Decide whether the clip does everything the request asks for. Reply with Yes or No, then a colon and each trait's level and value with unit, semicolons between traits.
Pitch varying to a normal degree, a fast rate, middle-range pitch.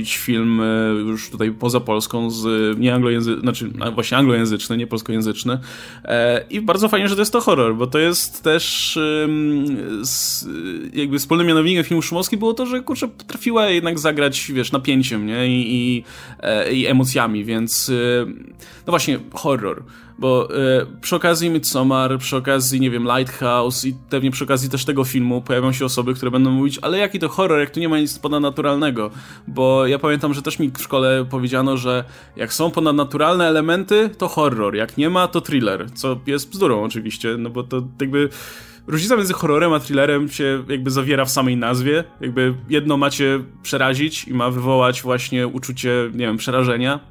No: average, 3.6 semitones; fast, 170 wpm; low, 130 Hz